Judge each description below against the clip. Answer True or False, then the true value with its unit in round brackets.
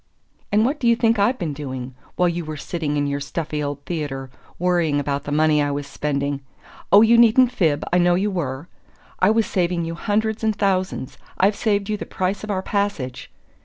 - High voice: False (175 Hz)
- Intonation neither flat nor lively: False (6.1 semitones)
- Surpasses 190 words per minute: True (205 wpm)